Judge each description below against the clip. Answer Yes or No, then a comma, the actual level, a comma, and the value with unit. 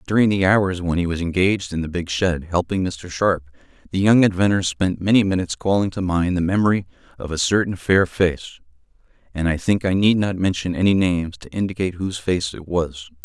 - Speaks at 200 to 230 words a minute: Yes, fast, 205 wpm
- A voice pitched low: Yes, very low, 90 Hz